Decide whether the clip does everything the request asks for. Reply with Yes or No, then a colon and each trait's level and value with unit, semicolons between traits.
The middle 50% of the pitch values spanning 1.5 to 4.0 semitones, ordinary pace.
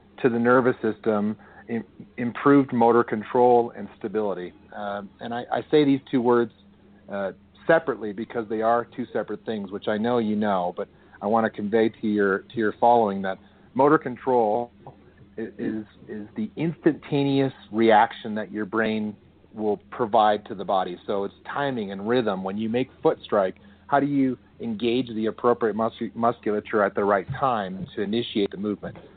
Yes: average, 2.8 semitones; average, 170 wpm